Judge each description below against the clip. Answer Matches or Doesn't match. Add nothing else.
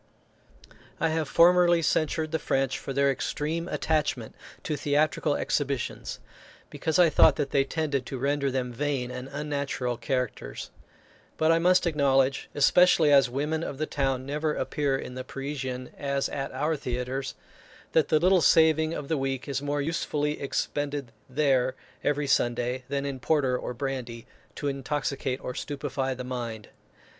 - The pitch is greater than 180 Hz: Doesn't match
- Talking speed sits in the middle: Matches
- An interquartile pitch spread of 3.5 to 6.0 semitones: Doesn't match